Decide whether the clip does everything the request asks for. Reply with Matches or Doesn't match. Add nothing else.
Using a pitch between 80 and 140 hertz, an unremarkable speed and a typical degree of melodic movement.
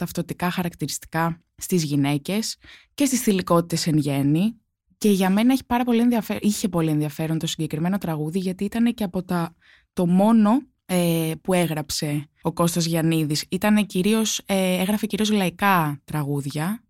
Doesn't match